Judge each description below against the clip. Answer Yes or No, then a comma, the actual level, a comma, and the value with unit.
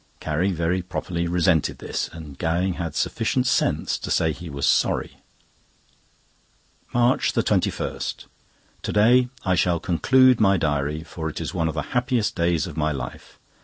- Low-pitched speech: Yes, very low, 85 Hz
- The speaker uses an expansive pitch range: No, average, 3.2 semitones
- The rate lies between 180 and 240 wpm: No, average, 150 wpm